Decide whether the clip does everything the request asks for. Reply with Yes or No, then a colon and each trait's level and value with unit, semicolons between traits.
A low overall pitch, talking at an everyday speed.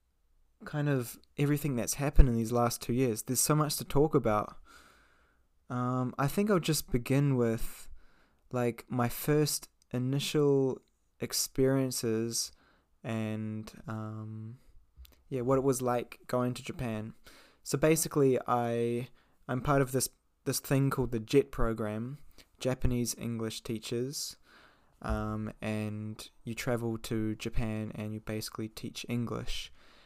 No: low, 120 Hz; slow, 130 wpm